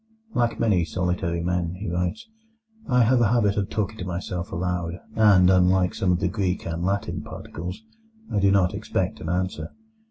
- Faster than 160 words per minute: Yes, average, 180 wpm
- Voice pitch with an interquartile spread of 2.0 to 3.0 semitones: Yes, narrow, 2.5 semitones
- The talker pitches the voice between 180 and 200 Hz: No, very low, 90 Hz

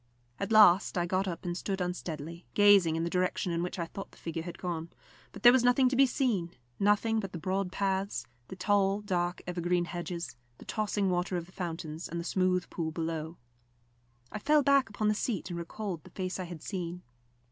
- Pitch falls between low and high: Yes, medium, 180 Hz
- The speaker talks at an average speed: No, fast, 210 wpm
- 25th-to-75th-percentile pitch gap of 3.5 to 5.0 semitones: No, average, 3.1 semitones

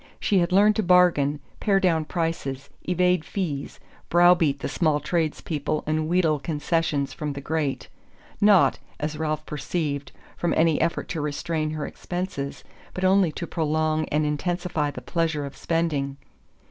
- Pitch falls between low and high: Yes, medium, 155 Hz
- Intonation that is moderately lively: Yes, average, 3.0 semitones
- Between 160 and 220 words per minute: No, average, 150 wpm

